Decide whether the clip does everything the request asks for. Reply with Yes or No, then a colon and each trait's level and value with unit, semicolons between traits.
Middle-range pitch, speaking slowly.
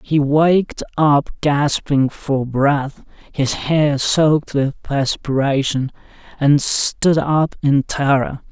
Yes: medium, 145 Hz; slow, 115 wpm